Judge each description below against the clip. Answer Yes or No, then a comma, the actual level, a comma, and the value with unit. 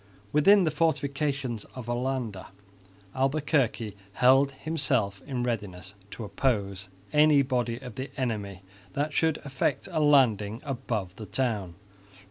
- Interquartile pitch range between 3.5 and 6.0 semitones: Yes, average, 5.0 semitones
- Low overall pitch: Yes, low, 130 Hz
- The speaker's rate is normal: No, slow, 120 wpm